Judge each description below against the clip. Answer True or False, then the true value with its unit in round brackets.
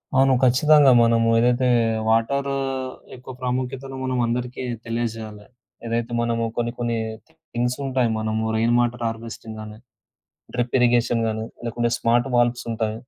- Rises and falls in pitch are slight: True (1.6 semitones)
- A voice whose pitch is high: False (120 Hz)